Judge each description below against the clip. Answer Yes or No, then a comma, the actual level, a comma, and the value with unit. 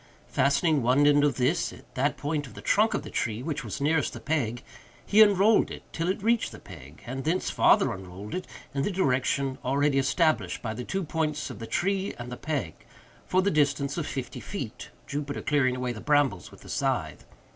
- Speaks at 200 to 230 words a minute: Yes, fast, 205 wpm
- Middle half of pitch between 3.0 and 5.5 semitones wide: Yes, average, 4.3 semitones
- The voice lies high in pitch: No, medium, 145 Hz